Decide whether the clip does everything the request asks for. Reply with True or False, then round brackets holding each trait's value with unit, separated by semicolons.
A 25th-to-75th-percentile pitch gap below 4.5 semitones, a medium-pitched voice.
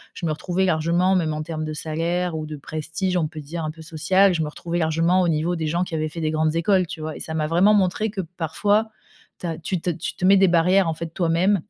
True (2.6 semitones; 165 Hz)